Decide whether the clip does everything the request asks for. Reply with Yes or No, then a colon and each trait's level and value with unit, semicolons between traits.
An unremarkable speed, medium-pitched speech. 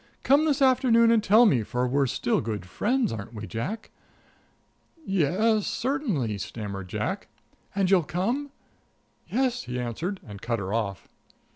Yes: average, 145 wpm; medium, 175 Hz